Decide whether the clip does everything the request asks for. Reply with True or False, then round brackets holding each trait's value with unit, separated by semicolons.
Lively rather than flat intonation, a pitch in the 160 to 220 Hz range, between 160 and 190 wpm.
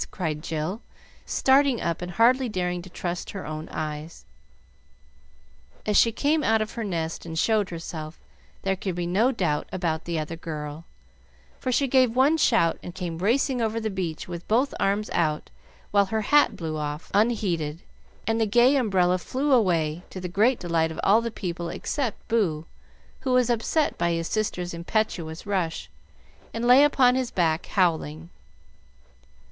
True (5.7 semitones; 185 Hz; 170 wpm)